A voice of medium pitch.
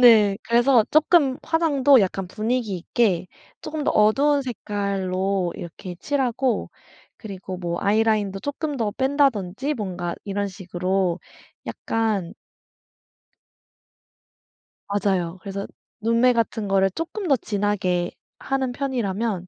No: high, 210 Hz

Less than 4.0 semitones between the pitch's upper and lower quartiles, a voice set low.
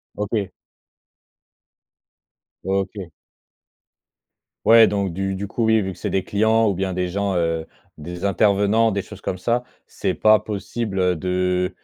Yes: average, 2.7 semitones; low, 100 Hz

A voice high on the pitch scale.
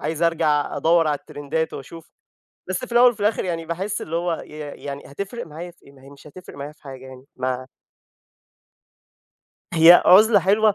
No: medium, 165 Hz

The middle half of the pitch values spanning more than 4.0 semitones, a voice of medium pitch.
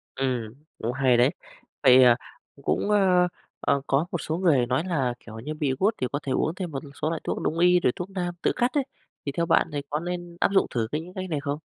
Yes: average, 5.2 semitones; medium, 155 Hz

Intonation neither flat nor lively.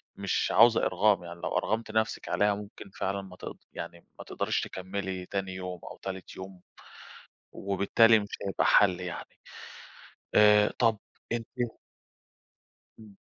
No: narrow, 2.2 semitones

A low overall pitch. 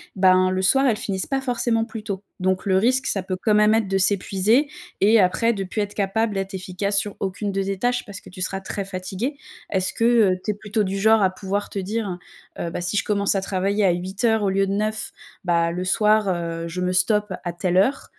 No: high, 195 Hz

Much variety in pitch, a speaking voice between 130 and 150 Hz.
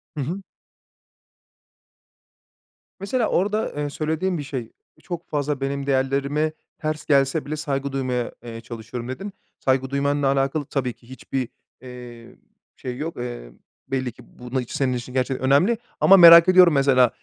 No: average, 3.3 semitones; low, 135 Hz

